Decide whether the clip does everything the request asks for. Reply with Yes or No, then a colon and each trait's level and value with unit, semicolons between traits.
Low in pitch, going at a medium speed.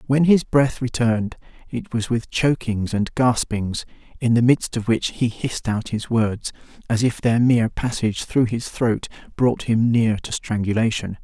Yes: low, 115 Hz; average, 175 wpm